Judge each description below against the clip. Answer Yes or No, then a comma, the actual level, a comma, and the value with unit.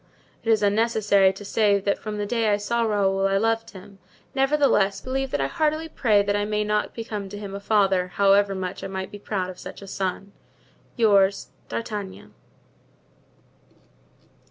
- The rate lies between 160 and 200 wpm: Yes, average, 175 wpm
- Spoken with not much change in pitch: Yes, narrow, 2.3 semitones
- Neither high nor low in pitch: No, high, 205 Hz